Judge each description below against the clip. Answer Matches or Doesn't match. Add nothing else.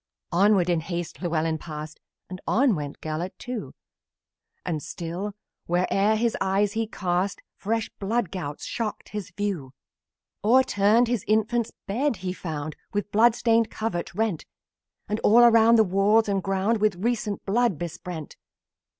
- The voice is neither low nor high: Doesn't match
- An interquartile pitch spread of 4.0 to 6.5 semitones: Matches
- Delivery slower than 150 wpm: Matches